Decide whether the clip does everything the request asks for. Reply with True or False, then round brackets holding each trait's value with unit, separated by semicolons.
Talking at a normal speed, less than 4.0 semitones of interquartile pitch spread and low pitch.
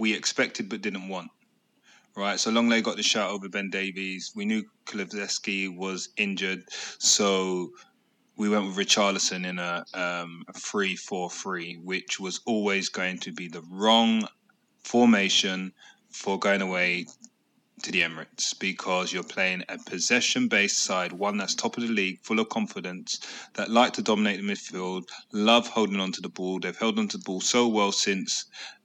True (170 wpm; 3.6 semitones; 100 Hz)